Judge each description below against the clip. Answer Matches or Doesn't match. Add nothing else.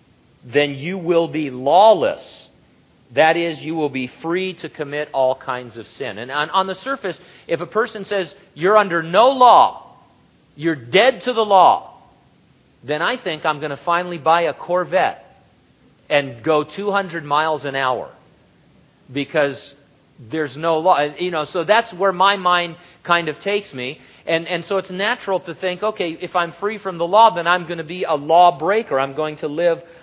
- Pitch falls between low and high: Matches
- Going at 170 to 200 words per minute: Matches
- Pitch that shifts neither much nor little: Matches